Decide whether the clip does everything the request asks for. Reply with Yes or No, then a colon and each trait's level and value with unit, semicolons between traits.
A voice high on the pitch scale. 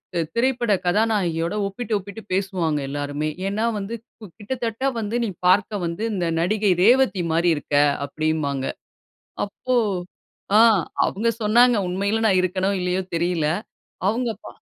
Yes: high, 195 Hz